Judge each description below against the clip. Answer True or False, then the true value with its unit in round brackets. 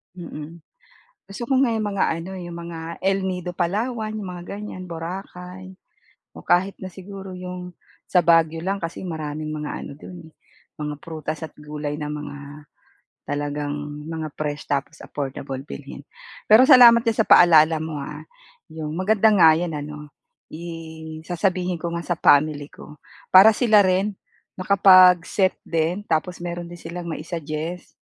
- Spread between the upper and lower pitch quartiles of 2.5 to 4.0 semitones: True (3.3 semitones)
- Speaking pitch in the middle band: True (170 Hz)